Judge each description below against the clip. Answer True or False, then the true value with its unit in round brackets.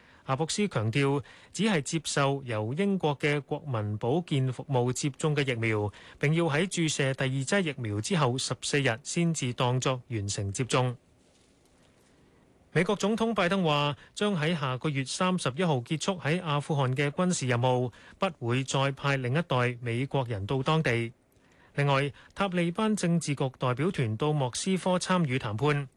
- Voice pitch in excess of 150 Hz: False (140 Hz)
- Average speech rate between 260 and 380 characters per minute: False (245 characters per minute)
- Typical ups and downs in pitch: True (4.6 semitones)